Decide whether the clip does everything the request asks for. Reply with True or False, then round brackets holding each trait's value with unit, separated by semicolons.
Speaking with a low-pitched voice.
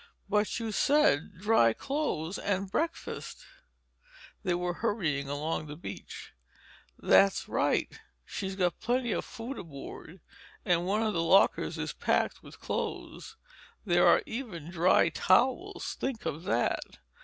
False (195 Hz)